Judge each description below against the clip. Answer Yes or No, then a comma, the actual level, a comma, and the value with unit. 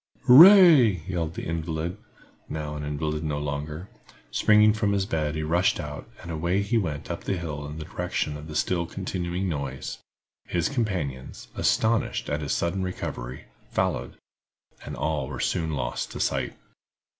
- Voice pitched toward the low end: Yes, very low, 80 Hz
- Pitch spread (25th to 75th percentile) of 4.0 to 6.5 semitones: Yes, average, 4.3 semitones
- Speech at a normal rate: Yes, average, 160 wpm